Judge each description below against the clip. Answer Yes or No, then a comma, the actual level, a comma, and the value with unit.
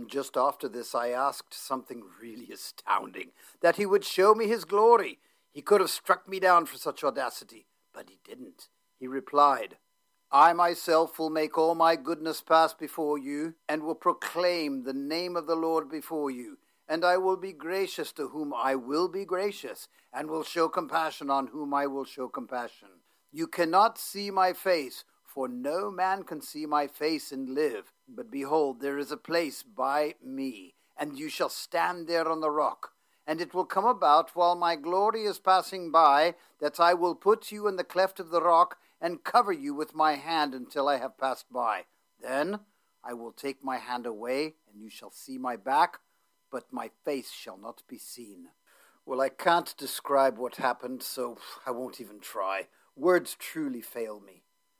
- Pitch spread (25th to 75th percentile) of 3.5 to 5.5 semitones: Yes, average, 4.9 semitones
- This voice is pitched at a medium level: Yes, medium, 160 Hz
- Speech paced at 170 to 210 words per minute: Yes, average, 185 wpm